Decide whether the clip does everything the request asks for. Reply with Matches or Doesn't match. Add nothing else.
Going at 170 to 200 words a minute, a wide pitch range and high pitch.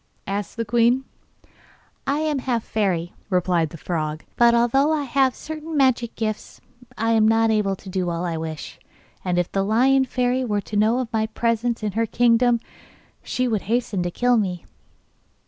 Doesn't match